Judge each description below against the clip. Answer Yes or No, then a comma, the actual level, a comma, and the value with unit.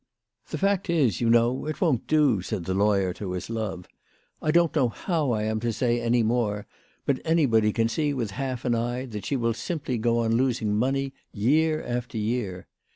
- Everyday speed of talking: No, fast, 215 wpm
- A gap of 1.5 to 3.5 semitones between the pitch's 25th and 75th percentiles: No, average, 4.0 semitones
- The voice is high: No, low, 120 Hz